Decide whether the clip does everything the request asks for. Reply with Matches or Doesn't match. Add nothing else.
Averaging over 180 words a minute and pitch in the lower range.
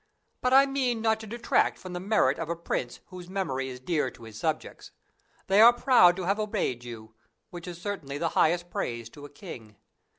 Doesn't match